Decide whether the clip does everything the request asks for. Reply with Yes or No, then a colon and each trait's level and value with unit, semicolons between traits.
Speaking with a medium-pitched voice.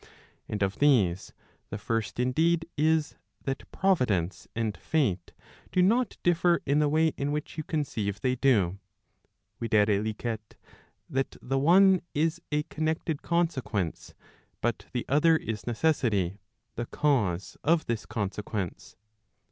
No: low, 130 Hz